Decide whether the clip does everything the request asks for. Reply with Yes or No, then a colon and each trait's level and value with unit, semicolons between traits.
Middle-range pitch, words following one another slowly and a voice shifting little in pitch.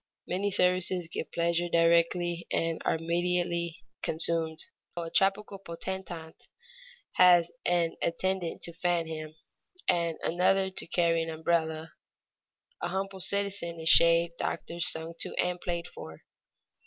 Yes: medium, 170 Hz; slow, 125 wpm; narrow, 1.5 semitones